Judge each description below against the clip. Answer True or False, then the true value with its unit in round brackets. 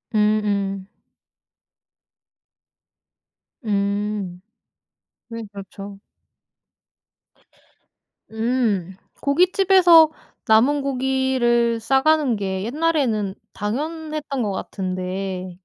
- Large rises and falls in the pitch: True (6.0 semitones)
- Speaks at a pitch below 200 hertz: False (225 Hz)